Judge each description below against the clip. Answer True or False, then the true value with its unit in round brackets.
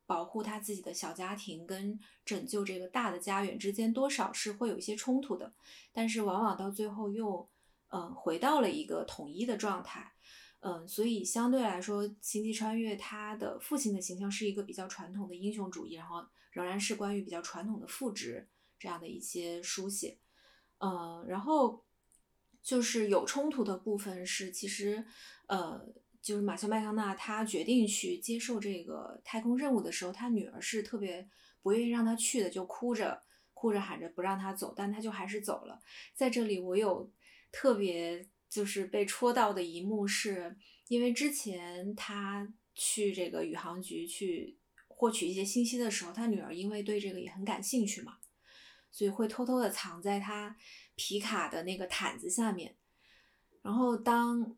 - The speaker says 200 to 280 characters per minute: True (270 characters per minute)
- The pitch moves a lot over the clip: False (3.0 semitones)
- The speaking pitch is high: True (210 Hz)